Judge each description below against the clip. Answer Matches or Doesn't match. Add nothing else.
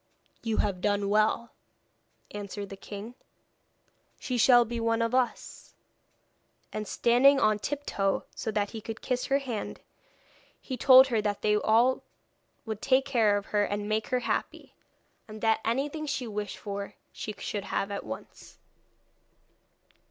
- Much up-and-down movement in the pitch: Doesn't match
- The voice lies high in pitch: Matches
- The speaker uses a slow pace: Doesn't match